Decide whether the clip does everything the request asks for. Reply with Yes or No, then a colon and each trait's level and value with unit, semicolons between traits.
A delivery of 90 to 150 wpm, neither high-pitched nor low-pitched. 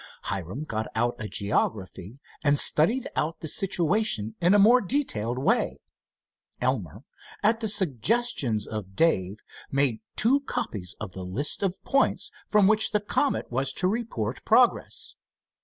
Yes: average, 140 wpm; medium, 145 Hz